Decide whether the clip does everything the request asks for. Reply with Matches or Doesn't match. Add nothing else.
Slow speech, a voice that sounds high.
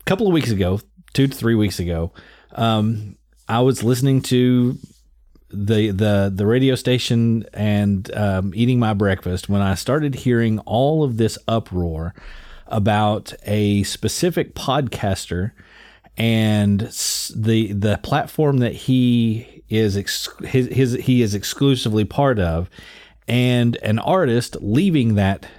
Doesn't match